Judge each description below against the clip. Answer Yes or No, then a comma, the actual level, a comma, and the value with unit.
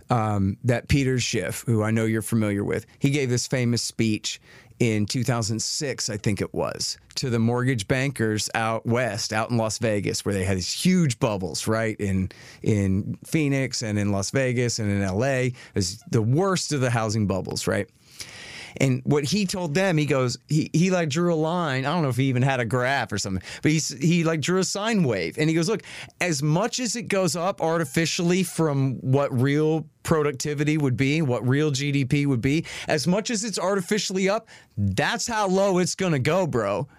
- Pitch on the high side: No, low, 135 Hz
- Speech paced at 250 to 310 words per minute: No, average, 200 wpm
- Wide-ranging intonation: Yes, wide, 6.4 semitones